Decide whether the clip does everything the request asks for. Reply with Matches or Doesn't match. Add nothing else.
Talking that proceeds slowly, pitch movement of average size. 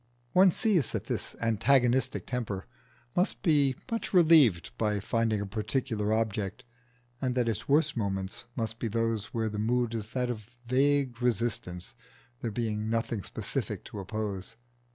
Doesn't match